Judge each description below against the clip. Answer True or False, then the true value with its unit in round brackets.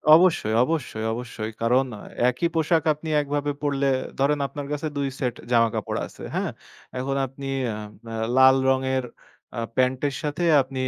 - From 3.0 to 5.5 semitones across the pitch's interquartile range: False (2.6 semitones)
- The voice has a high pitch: False (135 Hz)